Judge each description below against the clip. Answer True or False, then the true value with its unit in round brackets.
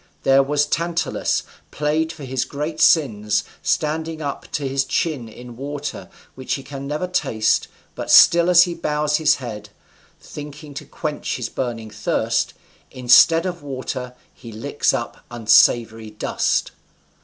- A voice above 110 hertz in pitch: True (140 Hz)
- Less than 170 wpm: True (145 wpm)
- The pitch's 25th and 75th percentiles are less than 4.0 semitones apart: False (4.3 semitones)